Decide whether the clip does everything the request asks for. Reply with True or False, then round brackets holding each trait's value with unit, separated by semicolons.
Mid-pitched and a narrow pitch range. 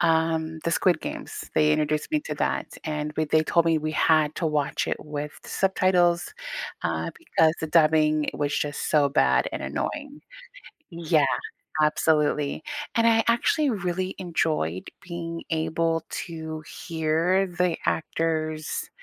True (160 Hz; 2.2 semitones)